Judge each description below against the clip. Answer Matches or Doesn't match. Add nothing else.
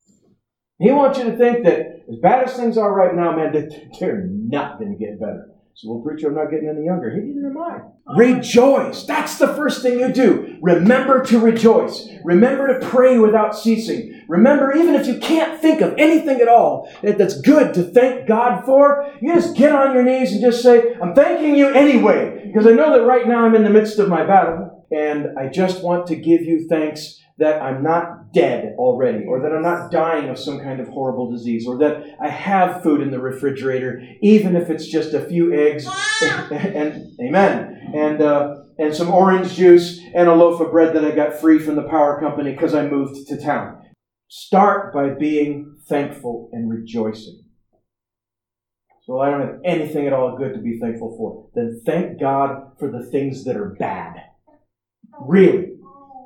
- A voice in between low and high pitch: Matches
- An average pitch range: Doesn't match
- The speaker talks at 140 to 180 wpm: Doesn't match